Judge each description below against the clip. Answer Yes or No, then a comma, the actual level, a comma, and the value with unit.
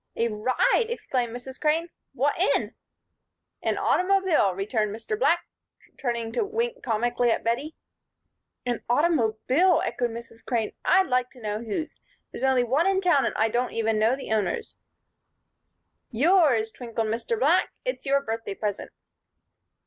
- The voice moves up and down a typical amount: No, wide, 6.4 semitones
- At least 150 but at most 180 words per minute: No, average, 140 wpm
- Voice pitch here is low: No, high, 245 Hz